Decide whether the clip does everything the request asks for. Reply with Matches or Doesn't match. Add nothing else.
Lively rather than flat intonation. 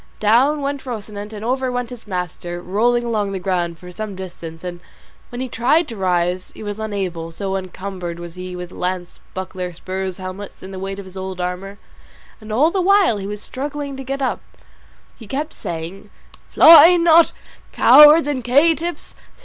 Matches